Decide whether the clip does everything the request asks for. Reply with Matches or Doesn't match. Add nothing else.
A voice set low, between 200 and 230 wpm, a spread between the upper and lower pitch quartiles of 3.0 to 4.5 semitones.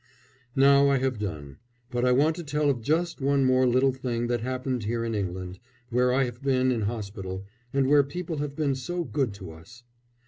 Matches